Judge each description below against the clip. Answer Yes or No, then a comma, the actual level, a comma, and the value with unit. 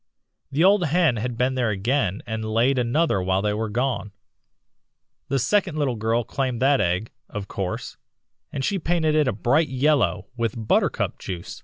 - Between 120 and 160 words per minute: No, average, 170 wpm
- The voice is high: No, low, 125 Hz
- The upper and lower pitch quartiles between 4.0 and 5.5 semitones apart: Yes, average, 5.0 semitones